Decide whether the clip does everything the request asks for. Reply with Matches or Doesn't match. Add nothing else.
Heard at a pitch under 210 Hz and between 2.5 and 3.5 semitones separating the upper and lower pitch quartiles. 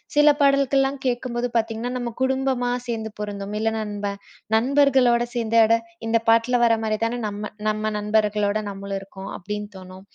Doesn't match